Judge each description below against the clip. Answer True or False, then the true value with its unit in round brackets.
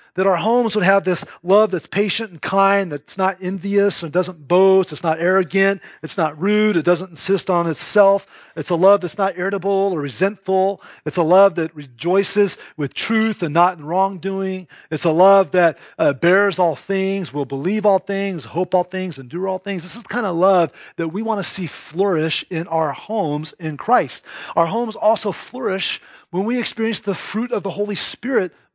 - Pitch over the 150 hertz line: True (190 Hz)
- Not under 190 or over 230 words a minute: True (200 wpm)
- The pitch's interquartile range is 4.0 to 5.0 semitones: False (2.8 semitones)